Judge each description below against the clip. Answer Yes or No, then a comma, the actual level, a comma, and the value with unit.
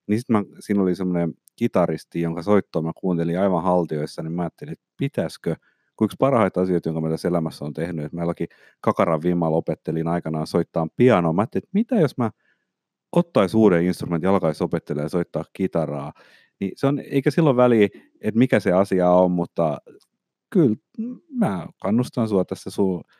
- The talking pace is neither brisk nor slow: No, fast, 175 wpm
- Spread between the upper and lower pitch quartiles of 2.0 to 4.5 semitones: No, average, 4.9 semitones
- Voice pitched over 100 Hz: No, very low, 90 Hz